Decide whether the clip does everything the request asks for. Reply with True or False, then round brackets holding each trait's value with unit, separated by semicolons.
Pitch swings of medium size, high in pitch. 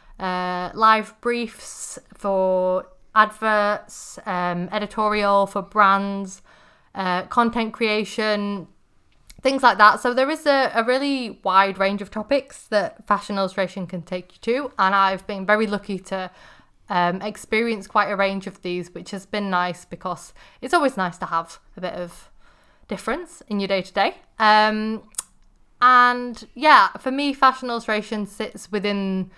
True (3.3 semitones; 210 Hz)